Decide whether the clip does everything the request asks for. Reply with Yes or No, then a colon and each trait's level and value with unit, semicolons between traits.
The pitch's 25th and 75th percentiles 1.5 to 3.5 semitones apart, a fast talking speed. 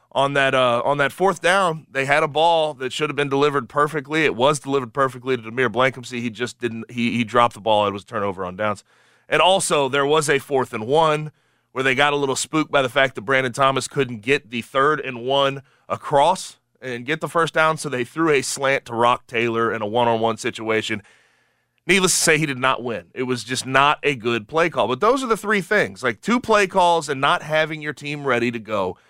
No: average, 4.1 semitones; fast, 235 wpm